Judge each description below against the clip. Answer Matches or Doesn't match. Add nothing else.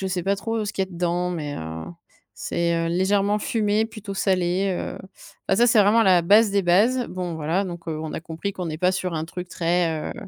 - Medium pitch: Matches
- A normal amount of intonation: Matches